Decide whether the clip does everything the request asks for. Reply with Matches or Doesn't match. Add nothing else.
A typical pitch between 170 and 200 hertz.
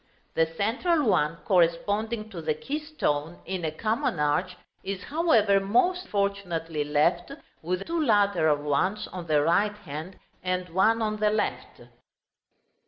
Matches